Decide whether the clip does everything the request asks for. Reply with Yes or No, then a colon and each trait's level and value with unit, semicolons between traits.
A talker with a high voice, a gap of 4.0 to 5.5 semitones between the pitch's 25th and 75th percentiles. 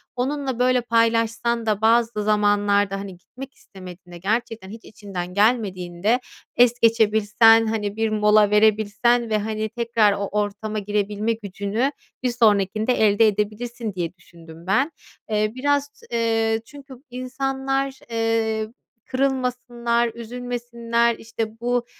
No: high, 225 Hz; narrow, 2.6 semitones